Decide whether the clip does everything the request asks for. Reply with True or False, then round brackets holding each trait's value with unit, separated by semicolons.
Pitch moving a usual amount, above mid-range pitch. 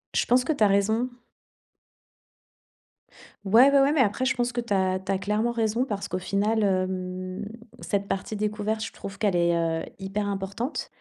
True (3.4 semitones; 205 Hz)